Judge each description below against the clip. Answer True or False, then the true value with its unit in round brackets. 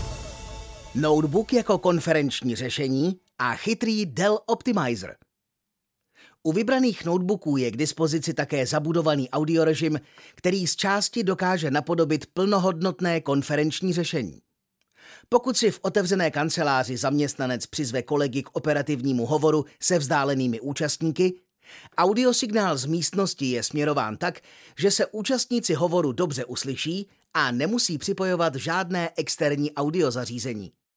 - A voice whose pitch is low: False (160 Hz)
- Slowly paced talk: True (110 wpm)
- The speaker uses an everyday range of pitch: True (4.9 semitones)